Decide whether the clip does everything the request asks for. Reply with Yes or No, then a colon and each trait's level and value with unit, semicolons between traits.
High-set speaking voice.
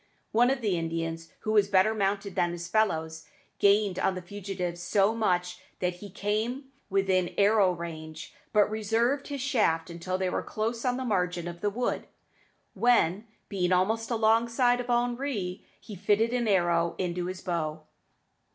Yes: high, 200 Hz